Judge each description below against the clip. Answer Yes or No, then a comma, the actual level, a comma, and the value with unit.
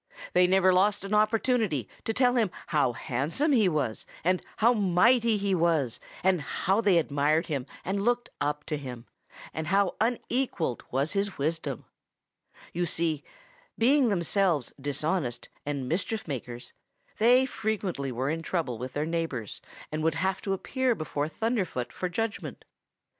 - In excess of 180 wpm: No, average, 150 wpm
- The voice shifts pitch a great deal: Yes, wide, 6.4 semitones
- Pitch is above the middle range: No, medium, 175 Hz